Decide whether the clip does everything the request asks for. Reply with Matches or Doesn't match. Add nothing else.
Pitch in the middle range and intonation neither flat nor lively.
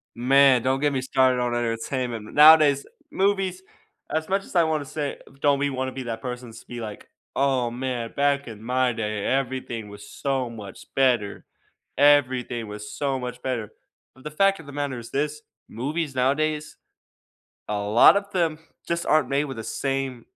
Doesn't match